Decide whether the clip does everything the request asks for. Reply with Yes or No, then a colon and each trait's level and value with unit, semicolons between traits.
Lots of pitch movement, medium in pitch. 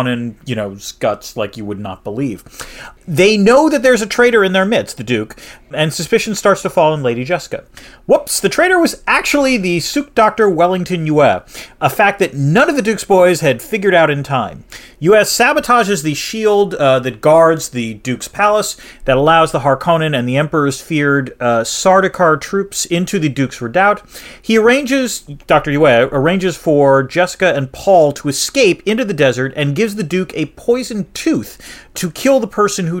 Yes: wide, 6.9 semitones; medium, 175 Hz